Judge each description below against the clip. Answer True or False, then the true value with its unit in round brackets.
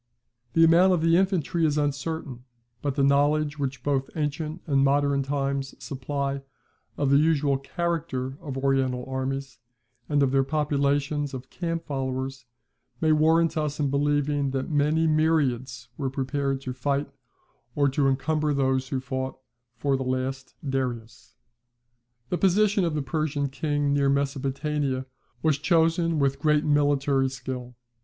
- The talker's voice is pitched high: False (140 Hz)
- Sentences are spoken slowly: False (145 wpm)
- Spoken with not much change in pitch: True (2.3 semitones)